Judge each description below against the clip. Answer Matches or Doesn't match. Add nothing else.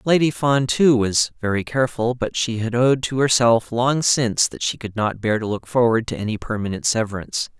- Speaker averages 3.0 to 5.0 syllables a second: Doesn't match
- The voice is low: Matches